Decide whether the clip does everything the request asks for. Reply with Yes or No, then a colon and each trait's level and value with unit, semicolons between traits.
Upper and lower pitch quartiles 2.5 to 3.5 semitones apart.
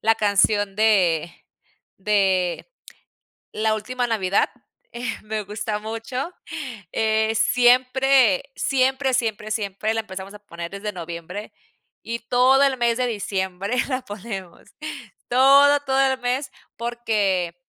No: average, 4.0 semitones